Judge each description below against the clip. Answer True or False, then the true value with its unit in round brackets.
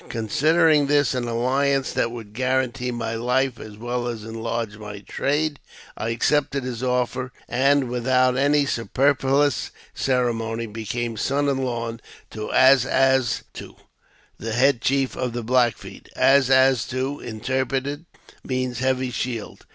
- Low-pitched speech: True (125 Hz)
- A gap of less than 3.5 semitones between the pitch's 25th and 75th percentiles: True (2.6 semitones)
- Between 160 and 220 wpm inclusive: False (140 wpm)